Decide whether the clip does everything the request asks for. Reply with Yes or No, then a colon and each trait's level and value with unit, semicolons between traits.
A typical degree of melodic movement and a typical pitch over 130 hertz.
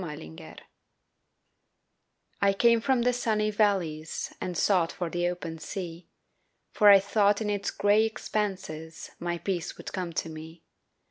Yes: average, 4.1 semitones; high, 190 Hz